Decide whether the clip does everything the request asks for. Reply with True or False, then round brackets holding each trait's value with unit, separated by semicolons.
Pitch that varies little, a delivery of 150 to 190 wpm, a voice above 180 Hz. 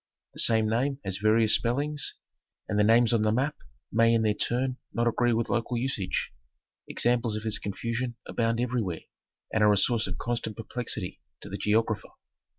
False (2.1 semitones; 175 wpm; 115 Hz)